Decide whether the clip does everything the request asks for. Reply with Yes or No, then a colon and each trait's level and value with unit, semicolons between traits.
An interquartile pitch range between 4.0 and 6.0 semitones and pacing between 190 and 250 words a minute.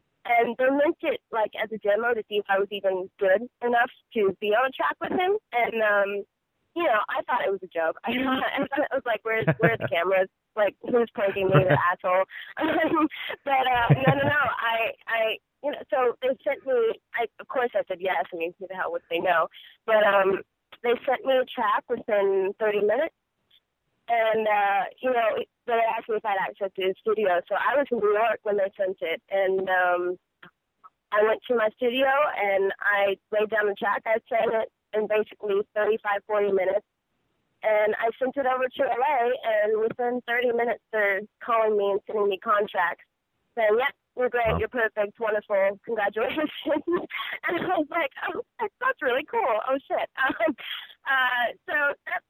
Yes: average, 4.8 semitones; average, 200 wpm